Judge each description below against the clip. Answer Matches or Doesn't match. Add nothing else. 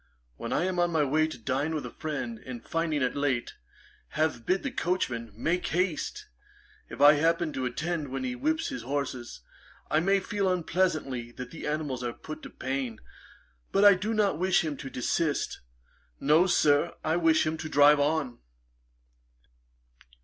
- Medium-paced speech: Matches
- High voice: Doesn't match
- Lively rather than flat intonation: Doesn't match